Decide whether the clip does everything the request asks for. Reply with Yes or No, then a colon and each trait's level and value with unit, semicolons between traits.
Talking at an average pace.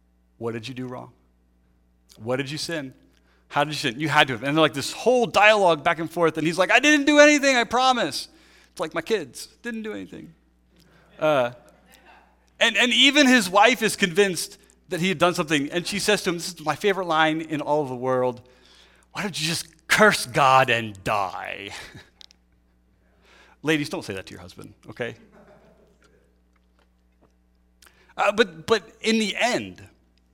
Yes: average, 180 wpm